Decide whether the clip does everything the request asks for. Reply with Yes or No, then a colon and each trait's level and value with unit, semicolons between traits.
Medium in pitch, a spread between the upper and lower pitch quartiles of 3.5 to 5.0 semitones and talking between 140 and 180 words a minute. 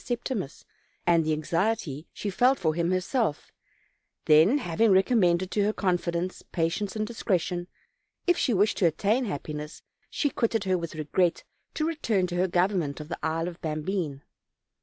Yes: medium, 180 Hz; average, 4.5 semitones; average, 160 wpm